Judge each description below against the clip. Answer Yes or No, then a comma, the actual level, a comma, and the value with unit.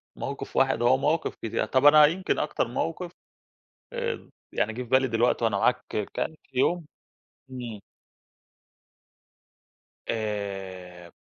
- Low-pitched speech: Yes, low, 125 Hz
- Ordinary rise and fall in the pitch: No, wide, 6.0 semitones